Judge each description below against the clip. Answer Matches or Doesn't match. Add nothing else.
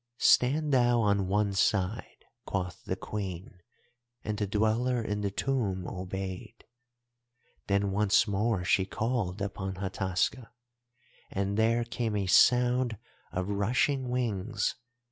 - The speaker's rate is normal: Doesn't match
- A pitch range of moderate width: Matches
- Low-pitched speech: Matches